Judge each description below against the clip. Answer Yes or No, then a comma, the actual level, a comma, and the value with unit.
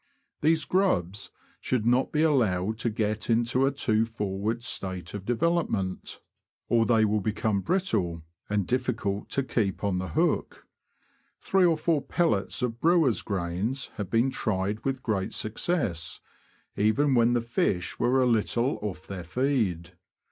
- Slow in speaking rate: No, average, 150 wpm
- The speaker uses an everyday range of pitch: Yes, average, 5.0 semitones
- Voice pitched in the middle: No, low, 115 Hz